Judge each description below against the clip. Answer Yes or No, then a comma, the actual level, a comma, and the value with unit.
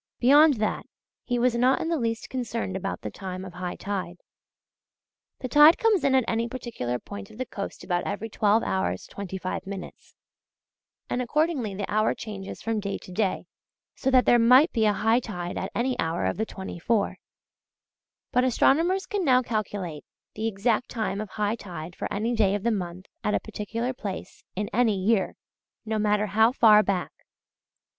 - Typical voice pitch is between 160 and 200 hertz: No, high, 215 Hz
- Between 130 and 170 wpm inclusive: No, average, 180 wpm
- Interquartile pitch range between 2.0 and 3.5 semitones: No, average, 4.0 semitones